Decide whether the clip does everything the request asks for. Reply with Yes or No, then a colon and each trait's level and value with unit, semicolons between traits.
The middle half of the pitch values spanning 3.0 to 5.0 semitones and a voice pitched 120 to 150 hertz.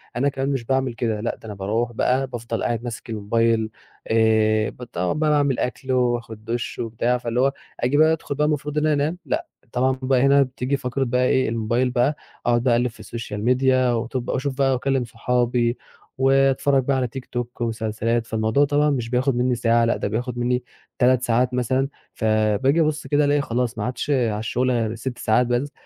No: narrow, 2.5 semitones; low, 125 Hz